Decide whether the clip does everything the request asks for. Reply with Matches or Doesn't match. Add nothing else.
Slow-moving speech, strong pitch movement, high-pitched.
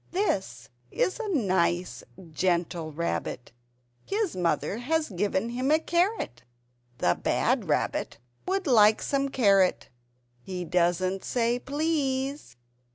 Matches